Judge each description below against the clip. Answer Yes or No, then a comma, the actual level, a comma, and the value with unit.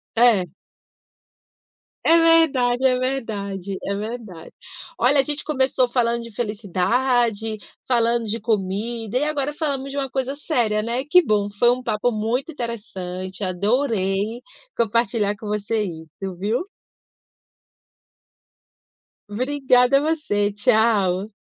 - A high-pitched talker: Yes, high, 230 Hz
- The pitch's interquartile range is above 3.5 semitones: Yes, average, 4.2 semitones